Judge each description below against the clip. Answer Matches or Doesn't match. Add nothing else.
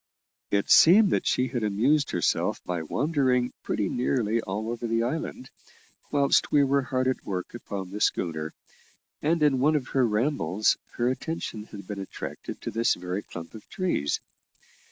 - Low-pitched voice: Matches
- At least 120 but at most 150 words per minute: Doesn't match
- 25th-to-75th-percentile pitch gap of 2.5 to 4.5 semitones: Doesn't match